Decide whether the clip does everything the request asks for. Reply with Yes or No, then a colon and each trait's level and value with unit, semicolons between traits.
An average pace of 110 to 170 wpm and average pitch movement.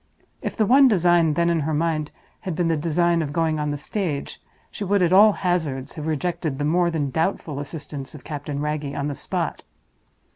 No: fast, 205 wpm; average, 3.0 semitones